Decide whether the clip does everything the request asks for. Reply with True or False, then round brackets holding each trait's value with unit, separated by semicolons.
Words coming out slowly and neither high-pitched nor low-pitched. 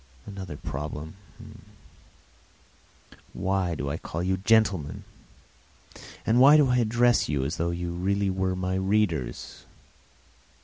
False (120 wpm; 95 Hz)